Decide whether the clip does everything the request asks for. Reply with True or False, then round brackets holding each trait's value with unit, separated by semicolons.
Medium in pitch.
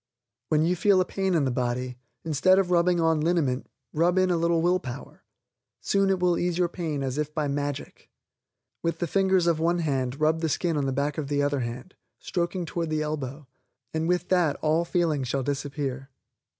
True (160 Hz)